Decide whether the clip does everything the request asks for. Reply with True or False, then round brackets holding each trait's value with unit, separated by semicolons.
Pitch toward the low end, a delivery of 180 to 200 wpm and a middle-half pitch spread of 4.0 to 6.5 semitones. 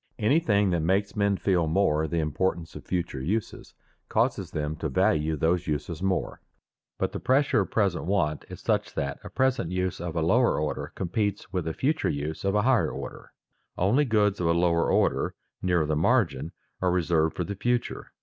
True (90 Hz; 190 wpm; 4.4 semitones)